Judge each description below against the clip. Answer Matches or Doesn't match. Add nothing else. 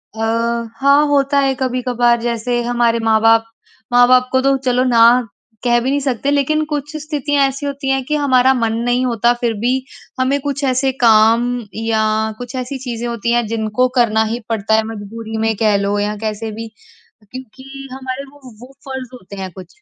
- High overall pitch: Matches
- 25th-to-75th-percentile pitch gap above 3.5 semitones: Doesn't match